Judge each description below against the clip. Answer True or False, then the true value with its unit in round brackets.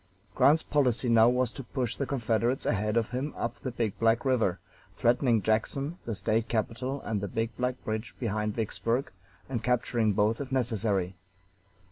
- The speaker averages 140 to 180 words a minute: True (165 wpm)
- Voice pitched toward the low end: True (115 Hz)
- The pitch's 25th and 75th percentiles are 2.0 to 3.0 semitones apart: True (2.6 semitones)